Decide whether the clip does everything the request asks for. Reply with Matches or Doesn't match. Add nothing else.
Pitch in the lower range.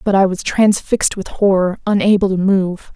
Doesn't match